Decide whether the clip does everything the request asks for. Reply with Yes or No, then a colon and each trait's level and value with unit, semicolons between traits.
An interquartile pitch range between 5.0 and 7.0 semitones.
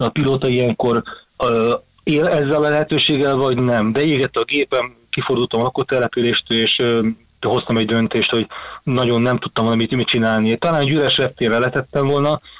No: average, 3.2 semitones